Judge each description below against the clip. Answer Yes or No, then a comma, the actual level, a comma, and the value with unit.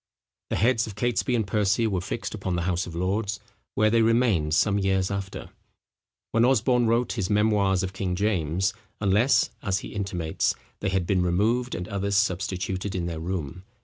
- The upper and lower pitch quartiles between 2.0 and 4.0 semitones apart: Yes, average, 3.1 semitones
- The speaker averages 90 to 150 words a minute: No, average, 180 wpm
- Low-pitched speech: Yes, low, 100 Hz